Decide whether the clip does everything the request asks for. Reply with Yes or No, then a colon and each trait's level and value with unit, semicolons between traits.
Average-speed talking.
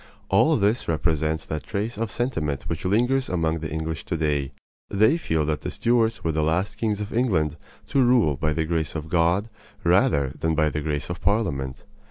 Yes: average, 195 wpm